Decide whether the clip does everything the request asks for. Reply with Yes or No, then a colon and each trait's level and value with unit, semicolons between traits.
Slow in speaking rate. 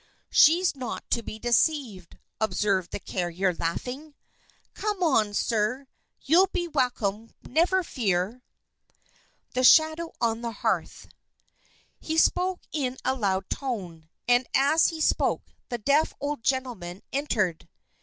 Yes: slow, 125 wpm